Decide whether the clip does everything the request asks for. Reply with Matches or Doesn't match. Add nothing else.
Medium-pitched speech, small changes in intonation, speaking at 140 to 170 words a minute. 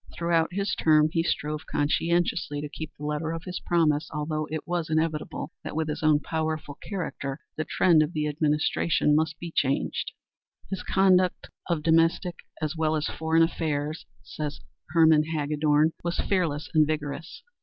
Matches